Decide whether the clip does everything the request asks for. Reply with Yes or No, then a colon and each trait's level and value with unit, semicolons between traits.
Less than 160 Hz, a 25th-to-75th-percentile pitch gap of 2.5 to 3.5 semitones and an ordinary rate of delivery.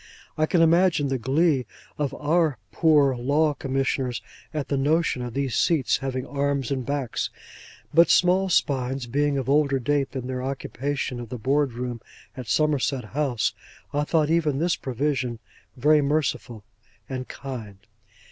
Yes: medium, 140 Hz; average, 2.8 semitones; average, 150 wpm